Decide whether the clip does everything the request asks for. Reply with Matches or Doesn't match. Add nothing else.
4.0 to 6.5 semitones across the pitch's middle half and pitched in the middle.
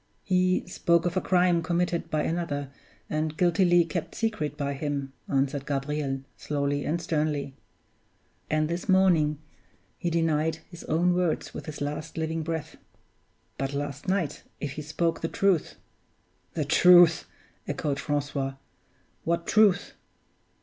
Doesn't match